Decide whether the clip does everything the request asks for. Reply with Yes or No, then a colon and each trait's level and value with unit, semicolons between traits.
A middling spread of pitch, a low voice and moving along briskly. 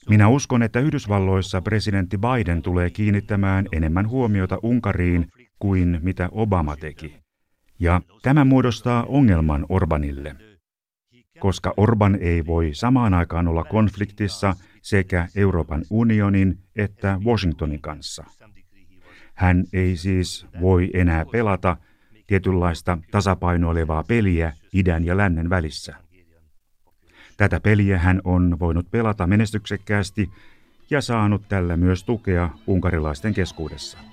No: average, 3.4 semitones; very low, 95 Hz; average, 105 wpm